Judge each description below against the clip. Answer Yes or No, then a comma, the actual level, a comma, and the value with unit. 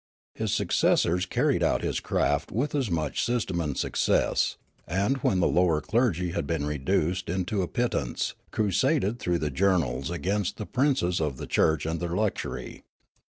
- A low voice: Yes, very low, 90 Hz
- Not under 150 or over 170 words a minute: Yes, average, 160 wpm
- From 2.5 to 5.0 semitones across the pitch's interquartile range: Yes, average, 4.5 semitones